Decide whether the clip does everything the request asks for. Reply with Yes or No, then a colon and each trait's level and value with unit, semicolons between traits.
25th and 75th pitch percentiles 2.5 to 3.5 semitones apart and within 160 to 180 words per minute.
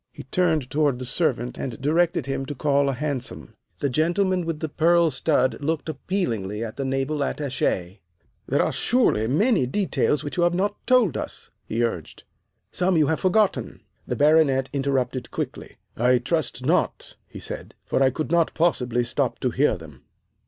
No: average, 4.7 semitones; average, 175 wpm